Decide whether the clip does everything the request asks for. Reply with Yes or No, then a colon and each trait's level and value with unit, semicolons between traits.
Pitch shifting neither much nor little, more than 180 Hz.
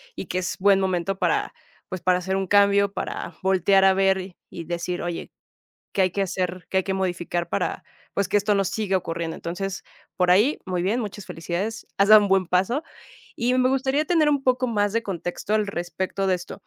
No: narrow, 2.2 semitones; high, 190 Hz